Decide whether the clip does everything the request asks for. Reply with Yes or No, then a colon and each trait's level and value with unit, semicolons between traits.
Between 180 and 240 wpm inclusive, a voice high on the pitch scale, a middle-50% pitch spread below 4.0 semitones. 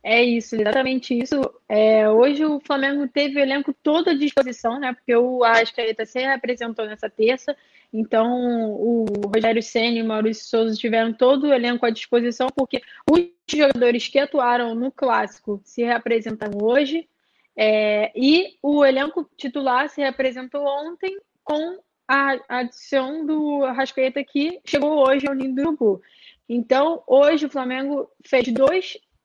No: average, 150 wpm; very high, 260 Hz; average, 3.6 semitones